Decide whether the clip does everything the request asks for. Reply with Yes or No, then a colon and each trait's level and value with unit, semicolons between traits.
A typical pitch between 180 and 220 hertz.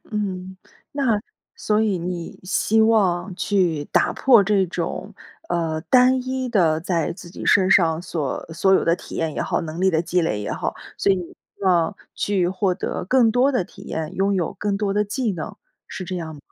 Yes: medium, 185 Hz